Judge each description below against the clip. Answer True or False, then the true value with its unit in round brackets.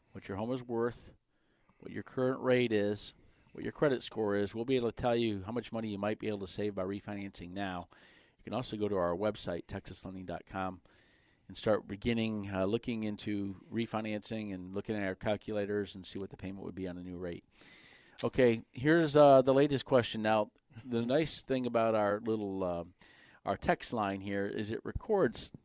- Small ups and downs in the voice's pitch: False (3.0 semitones)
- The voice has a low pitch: True (105 Hz)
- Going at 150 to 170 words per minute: False (200 wpm)